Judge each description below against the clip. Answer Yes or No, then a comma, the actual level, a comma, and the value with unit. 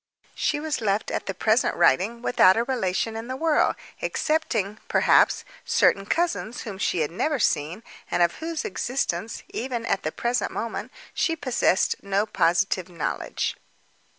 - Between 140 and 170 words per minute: Yes, average, 150 wpm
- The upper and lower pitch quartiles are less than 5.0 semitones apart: No, wide, 5.4 semitones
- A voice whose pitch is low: No, high, 225 Hz